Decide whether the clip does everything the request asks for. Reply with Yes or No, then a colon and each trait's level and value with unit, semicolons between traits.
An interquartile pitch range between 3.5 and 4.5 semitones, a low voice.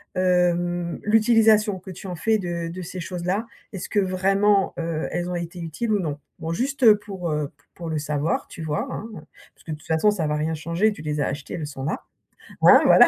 No: average, 3.9 semitones; medium, 175 Hz